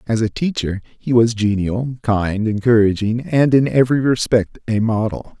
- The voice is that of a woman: No, male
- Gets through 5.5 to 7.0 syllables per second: No, 4.6 syllables/s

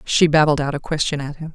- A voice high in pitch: No, medium, 150 Hz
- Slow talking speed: No, fast, 270 wpm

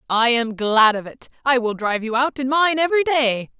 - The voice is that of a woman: Yes, female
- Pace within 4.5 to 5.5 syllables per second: Yes, 5.3 syllables/s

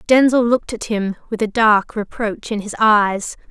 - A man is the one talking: No, female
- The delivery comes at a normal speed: Yes, average, 190 wpm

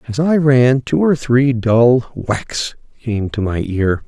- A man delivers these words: Yes, male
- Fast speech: No, average, 175 wpm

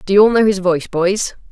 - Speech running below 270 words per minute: No, fast, 280 wpm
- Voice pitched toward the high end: Yes, high, 195 Hz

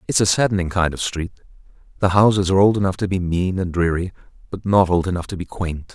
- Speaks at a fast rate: Yes, fast, 230 wpm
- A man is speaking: Yes, male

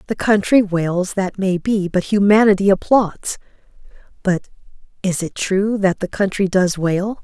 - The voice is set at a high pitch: Yes, high, 195 Hz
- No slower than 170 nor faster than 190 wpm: No, average, 150 wpm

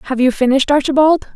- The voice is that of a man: No, female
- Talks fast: No, average, 175 wpm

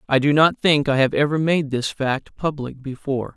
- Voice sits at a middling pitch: Yes, medium, 145 Hz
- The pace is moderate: No, fast, 215 wpm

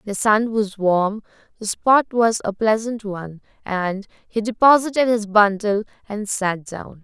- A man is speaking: No, female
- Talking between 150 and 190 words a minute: Yes, average, 155 wpm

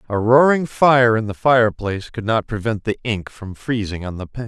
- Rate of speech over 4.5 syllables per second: Yes, 5.2 syllables/s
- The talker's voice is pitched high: No, low, 115 Hz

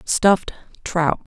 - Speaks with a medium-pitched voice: Yes, medium, 175 Hz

